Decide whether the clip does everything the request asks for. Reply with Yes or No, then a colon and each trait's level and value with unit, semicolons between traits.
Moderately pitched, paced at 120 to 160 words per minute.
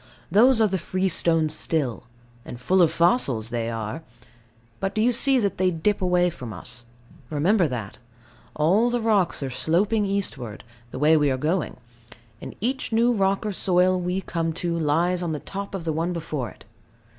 No: medium, 175 Hz; average, 180 wpm